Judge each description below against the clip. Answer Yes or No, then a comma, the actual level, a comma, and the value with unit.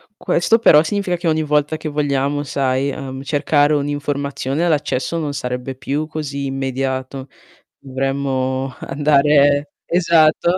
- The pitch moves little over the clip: Yes, narrow, 2.3 semitones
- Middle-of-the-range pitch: Yes, medium, 145 Hz